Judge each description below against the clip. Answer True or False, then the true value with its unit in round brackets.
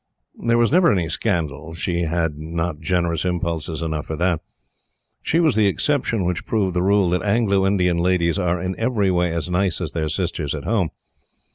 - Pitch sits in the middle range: False (90 Hz)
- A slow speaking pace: False (185 wpm)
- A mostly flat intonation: False (3.2 semitones)